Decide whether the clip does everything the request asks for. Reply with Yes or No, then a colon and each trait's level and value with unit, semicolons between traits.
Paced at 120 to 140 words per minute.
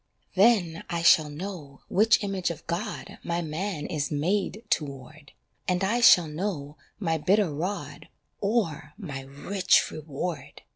Yes: slow, 135 wpm